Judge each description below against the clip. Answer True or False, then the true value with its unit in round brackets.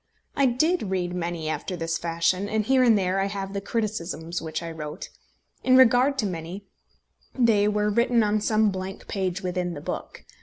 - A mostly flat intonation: False (3.9 semitones)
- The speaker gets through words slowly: False (185 wpm)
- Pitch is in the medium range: False (195 Hz)